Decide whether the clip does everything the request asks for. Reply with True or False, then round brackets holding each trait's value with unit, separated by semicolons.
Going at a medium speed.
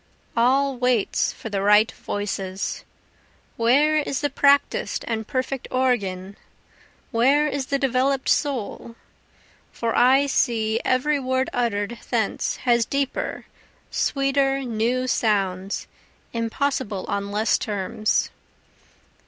False (105 wpm)